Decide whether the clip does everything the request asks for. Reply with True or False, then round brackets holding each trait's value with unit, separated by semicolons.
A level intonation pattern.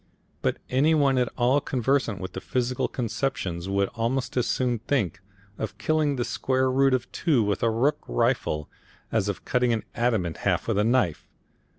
False (4.2 semitones)